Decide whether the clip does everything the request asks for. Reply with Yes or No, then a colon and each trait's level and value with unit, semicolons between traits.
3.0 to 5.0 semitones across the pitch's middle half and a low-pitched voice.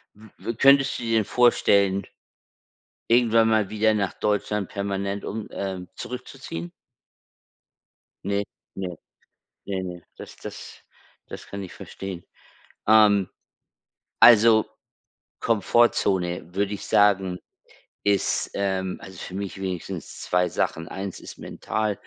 No: narrow, 2.5 semitones; low, 100 Hz